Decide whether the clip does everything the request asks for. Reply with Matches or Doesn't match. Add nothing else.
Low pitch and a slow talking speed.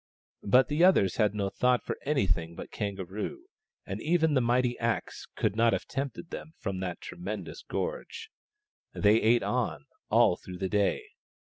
Doesn't match